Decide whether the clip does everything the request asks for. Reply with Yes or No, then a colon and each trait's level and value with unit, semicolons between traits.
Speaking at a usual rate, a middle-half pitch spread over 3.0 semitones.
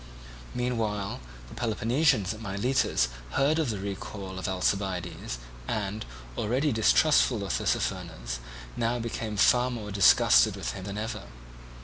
No: slow, 125 wpm; average, 3.7 semitones